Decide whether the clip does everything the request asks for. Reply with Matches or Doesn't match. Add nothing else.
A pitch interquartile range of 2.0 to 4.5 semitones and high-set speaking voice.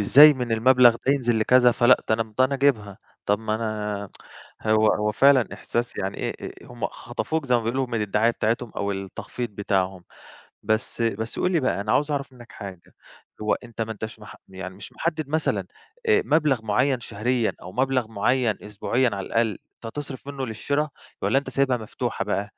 Doesn't match